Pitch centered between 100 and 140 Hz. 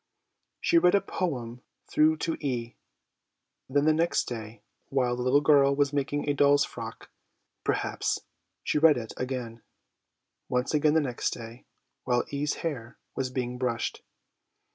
Yes: low, 135 Hz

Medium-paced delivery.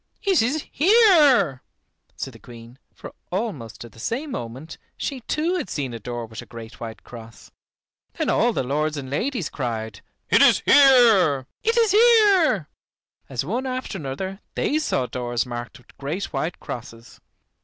Yes: average, 165 wpm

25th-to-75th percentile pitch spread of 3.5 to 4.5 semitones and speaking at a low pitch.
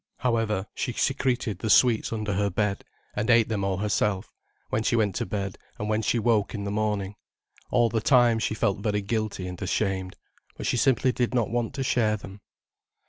No: average, 2.7 semitones; low, 110 Hz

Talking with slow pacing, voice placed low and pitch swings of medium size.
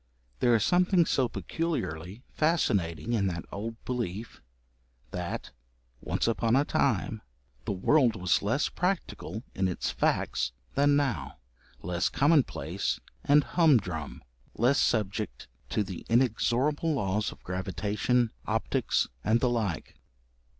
No: slow, 120 wpm; low, 115 Hz; wide, 6.6 semitones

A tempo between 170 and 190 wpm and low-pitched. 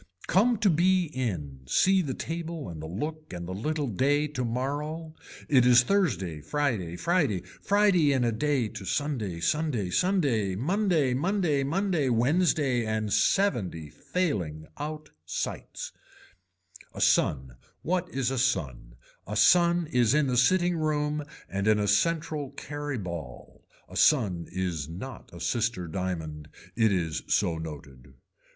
No: average, 140 wpm; low, 130 Hz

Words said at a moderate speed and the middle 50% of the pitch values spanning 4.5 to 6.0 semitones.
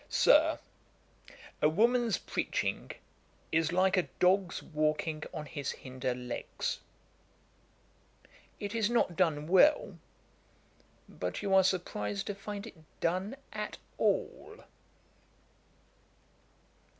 No: slow, 100 wpm; average, 5.2 semitones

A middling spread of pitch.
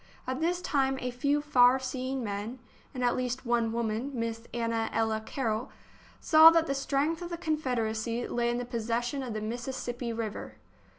Yes: average, 3.0 semitones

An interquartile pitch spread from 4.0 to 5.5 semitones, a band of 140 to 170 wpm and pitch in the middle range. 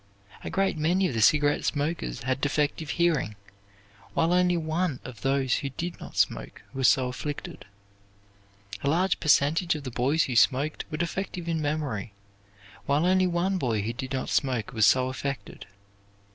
Yes: average, 4.6 semitones; average, 165 wpm; medium, 145 Hz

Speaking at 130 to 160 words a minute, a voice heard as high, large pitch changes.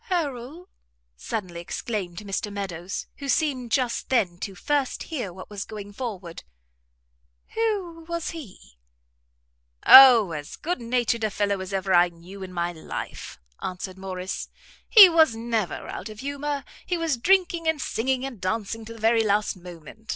Yes: average, 155 wpm; high, 225 Hz; wide, 6.8 semitones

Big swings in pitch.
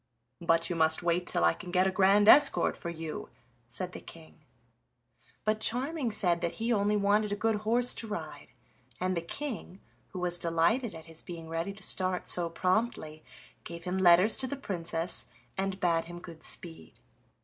No: average, 4.0 semitones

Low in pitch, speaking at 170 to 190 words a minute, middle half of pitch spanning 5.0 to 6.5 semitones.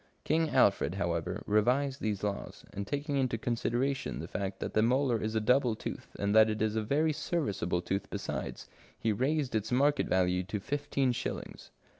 Yes: low, 115 Hz; average, 185 wpm; wide, 5.4 semitones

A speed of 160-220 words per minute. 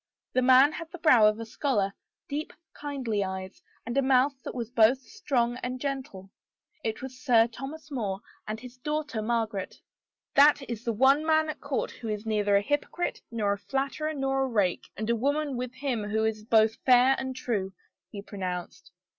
Yes: average, 190 wpm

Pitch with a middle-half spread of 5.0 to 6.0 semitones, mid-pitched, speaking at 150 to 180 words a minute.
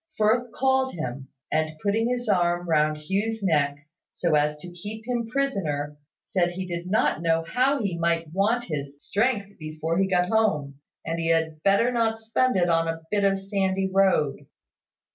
Yes: wide, 5.4 semitones; medium, 180 Hz; average, 175 wpm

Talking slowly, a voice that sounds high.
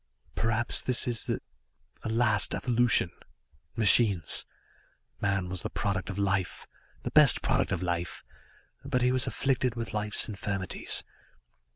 No: slow, 130 wpm; low, 105 Hz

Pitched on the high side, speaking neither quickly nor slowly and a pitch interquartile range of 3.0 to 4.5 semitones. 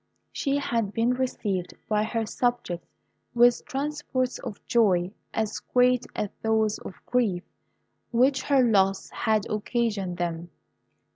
No: high, 225 Hz; slow, 125 wpm; average, 3.9 semitones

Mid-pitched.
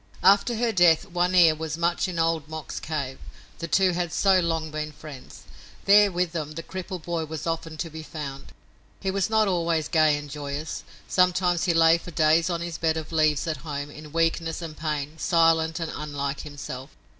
Yes: medium, 165 Hz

